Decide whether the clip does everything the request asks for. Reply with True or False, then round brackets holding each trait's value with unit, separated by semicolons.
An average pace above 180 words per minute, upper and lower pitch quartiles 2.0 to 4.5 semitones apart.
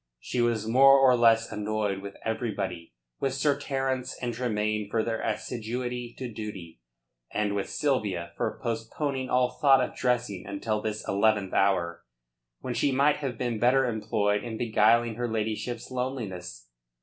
False (150 wpm; 3.1 semitones)